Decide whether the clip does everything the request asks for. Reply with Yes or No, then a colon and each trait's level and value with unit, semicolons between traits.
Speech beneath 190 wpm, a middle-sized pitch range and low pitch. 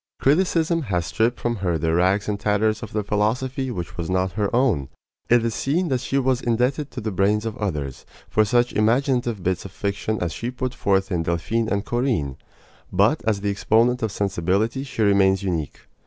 No: average, 195 wpm; average, 4.3 semitones; low, 105 Hz